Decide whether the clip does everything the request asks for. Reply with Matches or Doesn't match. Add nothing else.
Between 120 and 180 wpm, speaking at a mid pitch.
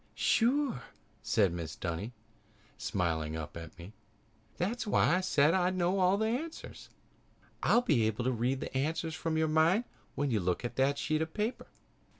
Matches